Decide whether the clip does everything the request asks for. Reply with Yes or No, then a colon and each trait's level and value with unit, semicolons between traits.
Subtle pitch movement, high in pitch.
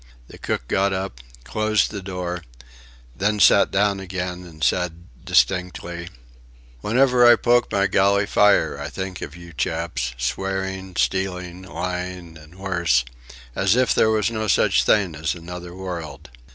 No: narrow, 2.3 semitones; very low, 95 Hz